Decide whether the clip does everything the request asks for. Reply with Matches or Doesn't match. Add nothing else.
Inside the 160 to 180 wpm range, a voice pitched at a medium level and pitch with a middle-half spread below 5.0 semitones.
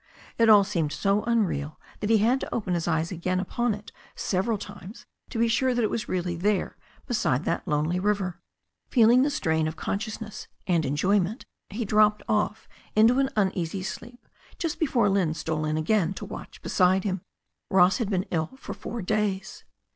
Doesn't match